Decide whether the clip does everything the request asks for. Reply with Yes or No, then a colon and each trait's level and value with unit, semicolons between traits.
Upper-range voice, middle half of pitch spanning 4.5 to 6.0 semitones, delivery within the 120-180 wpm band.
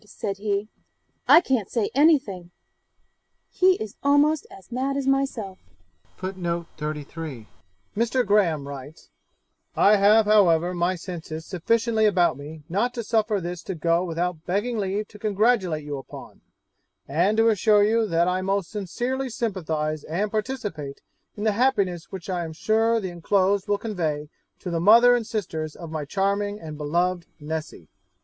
Yes: high, 195 Hz; average, 4.8 semitones; average, 150 wpm